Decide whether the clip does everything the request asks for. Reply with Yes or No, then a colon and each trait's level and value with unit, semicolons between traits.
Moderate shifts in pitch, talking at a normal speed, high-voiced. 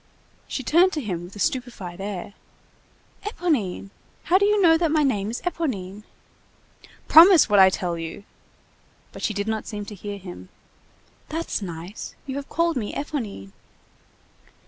No: wide, 8.5 semitones; average, 155 wpm; high, 215 Hz